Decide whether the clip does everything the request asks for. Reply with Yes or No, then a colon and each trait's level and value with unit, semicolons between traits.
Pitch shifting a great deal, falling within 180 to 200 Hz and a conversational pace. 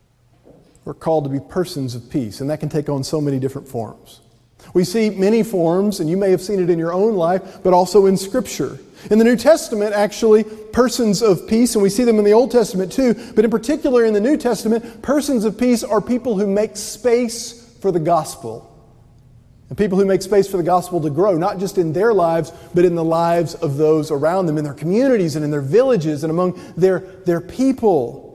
No: wide, 5.7 semitones; medium, 185 Hz; fast, 220 wpm